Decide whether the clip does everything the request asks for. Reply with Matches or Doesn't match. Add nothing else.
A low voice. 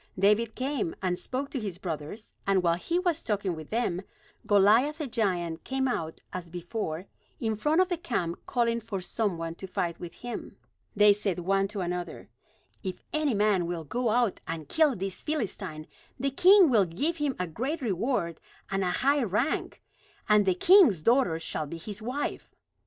Doesn't match